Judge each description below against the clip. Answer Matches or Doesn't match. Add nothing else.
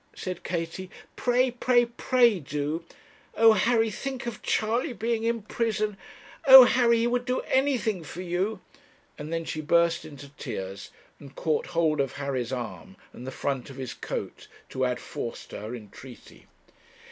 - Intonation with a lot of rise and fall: Matches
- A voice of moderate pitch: Matches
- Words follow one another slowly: Doesn't match